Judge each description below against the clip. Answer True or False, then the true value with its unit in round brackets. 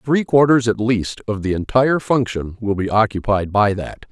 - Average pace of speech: True (190 wpm)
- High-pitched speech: False (110 Hz)